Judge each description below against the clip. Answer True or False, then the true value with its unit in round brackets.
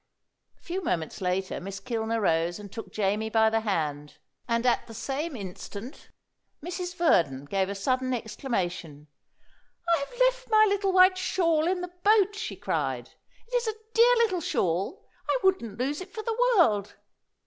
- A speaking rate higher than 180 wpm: False (165 wpm)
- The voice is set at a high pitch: True (250 Hz)